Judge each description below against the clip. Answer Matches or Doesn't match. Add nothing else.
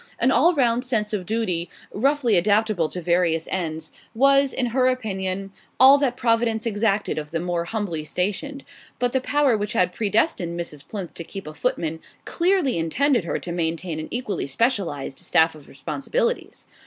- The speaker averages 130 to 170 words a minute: Matches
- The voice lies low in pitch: Doesn't match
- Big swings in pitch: Matches